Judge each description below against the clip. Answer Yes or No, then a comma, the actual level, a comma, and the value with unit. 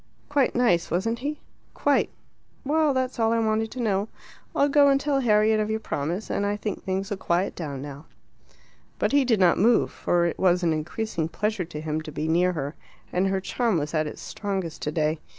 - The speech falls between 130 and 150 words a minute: No, fast, 205 wpm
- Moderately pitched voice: No, high, 195 Hz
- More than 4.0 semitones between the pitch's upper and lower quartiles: Yes, wide, 5.6 semitones